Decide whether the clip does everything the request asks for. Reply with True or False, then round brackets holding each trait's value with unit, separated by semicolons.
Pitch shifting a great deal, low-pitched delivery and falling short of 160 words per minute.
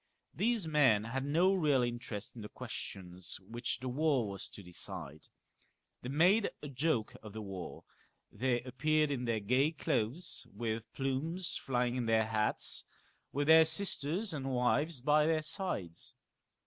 True (5.7 semitones; 130 Hz; 150 wpm)